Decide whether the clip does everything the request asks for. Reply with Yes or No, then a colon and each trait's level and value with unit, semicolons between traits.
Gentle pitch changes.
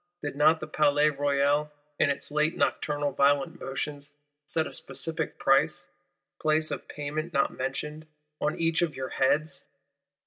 Yes: narrow, 1.6 semitones